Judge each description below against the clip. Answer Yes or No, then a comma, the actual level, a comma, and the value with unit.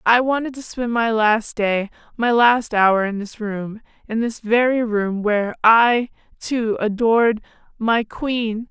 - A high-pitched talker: Yes, high, 225 Hz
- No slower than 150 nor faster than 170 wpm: Yes, average, 160 wpm